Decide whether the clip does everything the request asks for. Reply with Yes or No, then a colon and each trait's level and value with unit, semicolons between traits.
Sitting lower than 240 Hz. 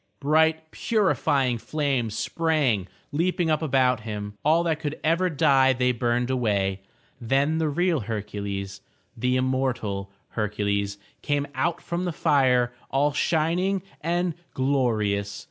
Yes: low, 135 Hz